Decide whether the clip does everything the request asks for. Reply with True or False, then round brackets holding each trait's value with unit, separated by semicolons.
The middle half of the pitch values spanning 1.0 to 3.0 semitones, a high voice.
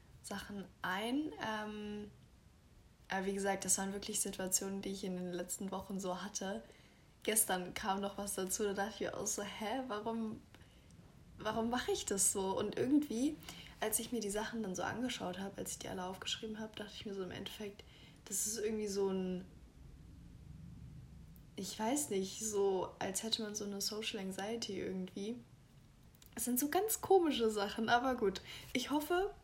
True (2.7 semitones; 205 Hz)